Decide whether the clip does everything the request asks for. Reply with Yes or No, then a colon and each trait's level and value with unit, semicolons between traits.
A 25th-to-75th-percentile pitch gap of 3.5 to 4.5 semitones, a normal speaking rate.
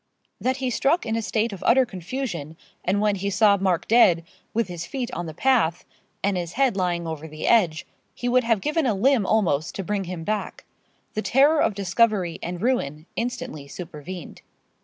No: wide, 5.5 semitones; average, 190 wpm